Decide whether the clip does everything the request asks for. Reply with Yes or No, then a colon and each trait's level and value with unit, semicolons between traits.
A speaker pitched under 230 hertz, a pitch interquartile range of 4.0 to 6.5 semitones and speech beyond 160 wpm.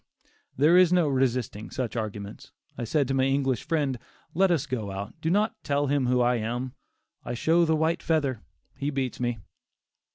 Yes: low, 135 Hz; average, 4.5 semitones; average, 185 wpm